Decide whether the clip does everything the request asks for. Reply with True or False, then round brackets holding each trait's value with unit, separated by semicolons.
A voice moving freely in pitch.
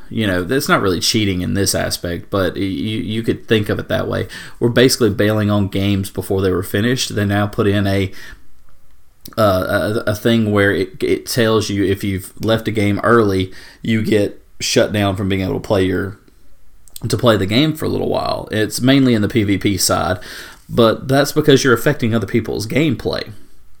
False (3.1 semitones)